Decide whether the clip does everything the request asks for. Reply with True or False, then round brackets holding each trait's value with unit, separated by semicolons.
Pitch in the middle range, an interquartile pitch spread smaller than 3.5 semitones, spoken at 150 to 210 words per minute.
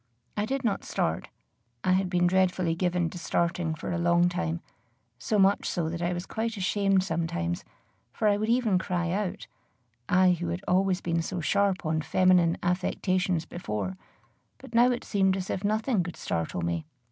True (180 Hz; 2.5 semitones; 180 wpm)